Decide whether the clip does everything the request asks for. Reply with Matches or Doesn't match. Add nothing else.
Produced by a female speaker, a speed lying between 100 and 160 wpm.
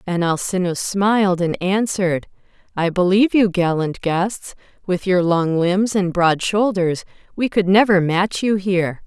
Matches